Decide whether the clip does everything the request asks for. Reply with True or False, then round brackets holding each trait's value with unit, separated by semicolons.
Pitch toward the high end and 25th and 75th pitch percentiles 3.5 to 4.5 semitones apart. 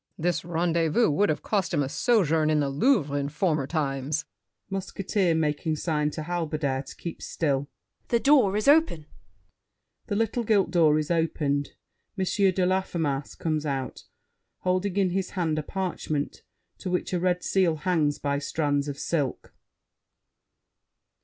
False (165 Hz; 4.0 semitones)